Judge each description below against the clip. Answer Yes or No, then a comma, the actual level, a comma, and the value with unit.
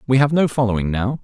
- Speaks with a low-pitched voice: Yes, low, 125 Hz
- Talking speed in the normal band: Yes, average, 195 wpm